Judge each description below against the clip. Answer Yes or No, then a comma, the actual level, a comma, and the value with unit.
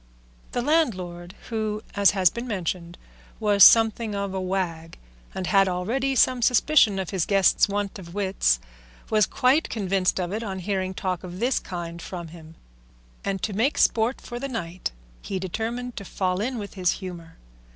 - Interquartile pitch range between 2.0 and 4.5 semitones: Yes, average, 3.7 semitones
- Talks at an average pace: Yes, average, 170 wpm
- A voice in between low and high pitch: No, high, 195 Hz